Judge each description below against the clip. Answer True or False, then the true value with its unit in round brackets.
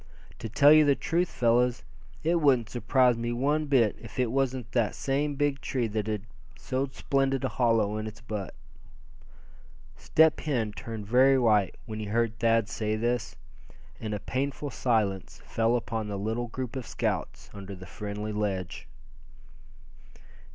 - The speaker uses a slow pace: False (160 wpm)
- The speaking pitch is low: True (115 Hz)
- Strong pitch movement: False (3.8 semitones)